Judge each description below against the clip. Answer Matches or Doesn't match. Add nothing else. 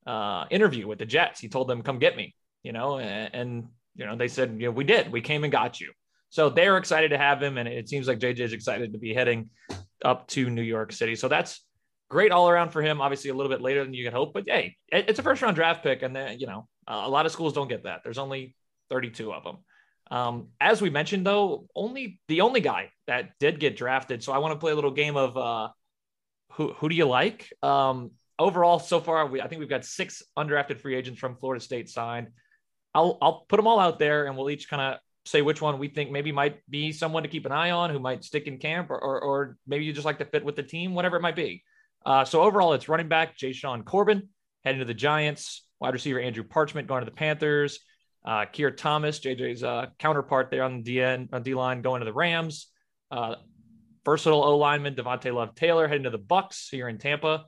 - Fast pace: Matches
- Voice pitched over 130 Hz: Matches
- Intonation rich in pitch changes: Doesn't match